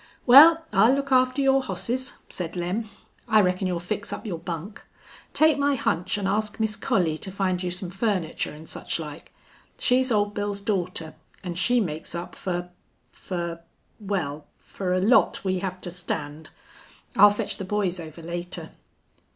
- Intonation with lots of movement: No, average, 3.9 semitones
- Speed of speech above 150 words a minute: Yes, average, 165 wpm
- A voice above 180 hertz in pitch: Yes, high, 190 Hz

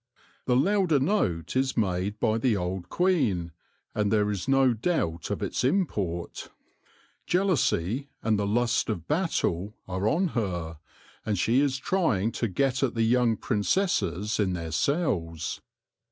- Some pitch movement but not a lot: No, wide, 6.6 semitones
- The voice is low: Yes, low, 110 Hz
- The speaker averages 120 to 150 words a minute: Yes, average, 145 wpm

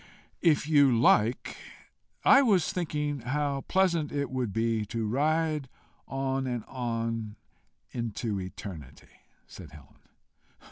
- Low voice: Yes, low, 130 Hz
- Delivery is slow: Yes, slow, 110 wpm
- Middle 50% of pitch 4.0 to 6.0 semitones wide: Yes, average, 4.6 semitones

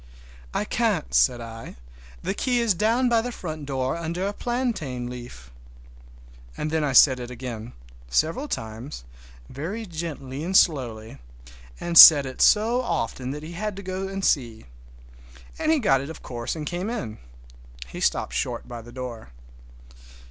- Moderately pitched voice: Yes, medium, 150 Hz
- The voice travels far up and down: Yes, wide, 7.9 semitones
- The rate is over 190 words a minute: No, average, 165 wpm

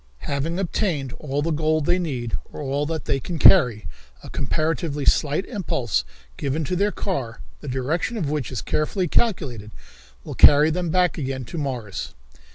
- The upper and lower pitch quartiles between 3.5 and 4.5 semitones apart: Yes, average, 4.2 semitones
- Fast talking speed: No, average, 165 wpm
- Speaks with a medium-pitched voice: Yes, medium, 150 Hz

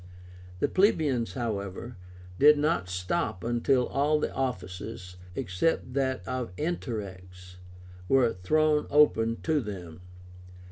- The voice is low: Yes, low, 120 Hz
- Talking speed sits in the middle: No, slow, 105 wpm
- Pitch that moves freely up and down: Yes, wide, 8.0 semitones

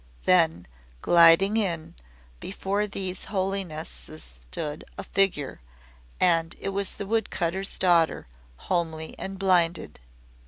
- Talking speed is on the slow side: Yes, slow, 110 wpm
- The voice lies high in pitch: No, medium, 175 Hz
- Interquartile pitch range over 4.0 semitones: No, average, 3.2 semitones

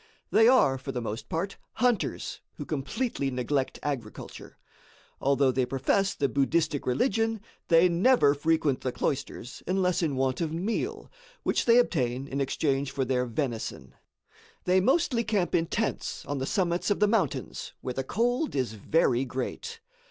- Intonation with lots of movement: Yes, wide, 6.9 semitones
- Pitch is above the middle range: No, medium, 145 Hz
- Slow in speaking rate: No, average, 155 wpm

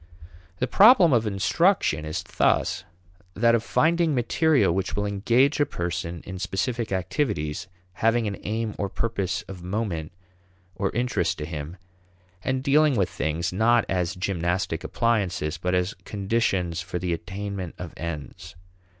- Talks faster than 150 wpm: No, average, 140 wpm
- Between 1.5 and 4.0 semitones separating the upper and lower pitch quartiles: No, average, 5.2 semitones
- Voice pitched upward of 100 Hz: No, very low, 95 Hz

